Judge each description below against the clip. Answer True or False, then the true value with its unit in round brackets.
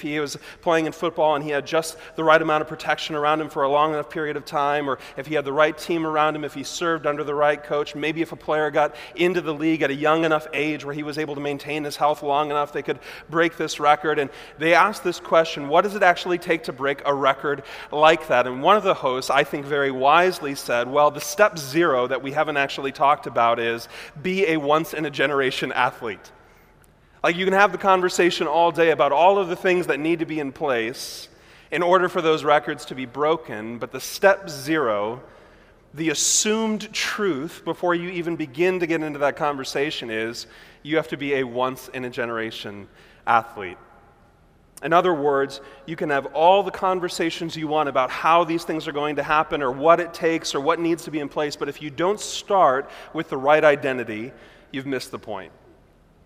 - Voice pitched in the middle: True (155 Hz)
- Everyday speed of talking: False (220 wpm)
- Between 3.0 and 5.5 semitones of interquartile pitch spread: False (2.6 semitones)